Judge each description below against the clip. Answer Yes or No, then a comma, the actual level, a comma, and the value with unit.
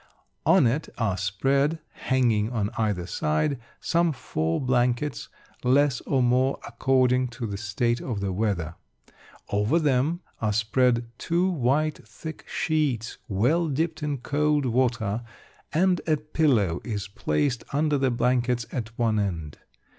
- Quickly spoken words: No, slow, 135 wpm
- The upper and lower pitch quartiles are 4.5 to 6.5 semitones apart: Yes, average, 5.2 semitones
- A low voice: Yes, low, 125 Hz